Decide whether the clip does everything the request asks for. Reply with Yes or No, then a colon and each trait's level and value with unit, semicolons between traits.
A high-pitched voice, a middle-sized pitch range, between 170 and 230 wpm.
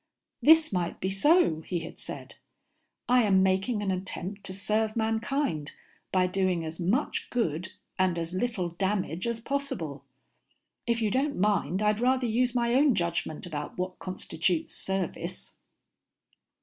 No: high, 195 Hz; average, 4.9 semitones; average, 145 wpm